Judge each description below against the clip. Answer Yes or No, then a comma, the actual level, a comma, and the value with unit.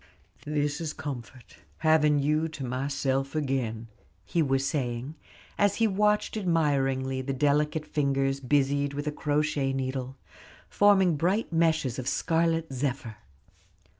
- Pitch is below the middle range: No, medium, 145 Hz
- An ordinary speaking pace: No, slow, 125 wpm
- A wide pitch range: No, average, 3.0 semitones